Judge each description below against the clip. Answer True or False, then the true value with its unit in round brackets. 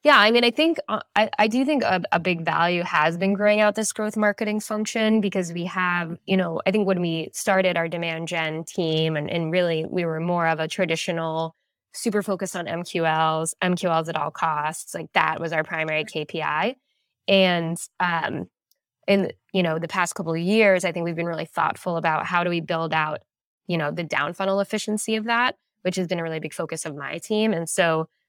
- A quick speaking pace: True (215 wpm)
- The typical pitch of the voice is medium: True (175 Hz)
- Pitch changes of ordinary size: True (4.0 semitones)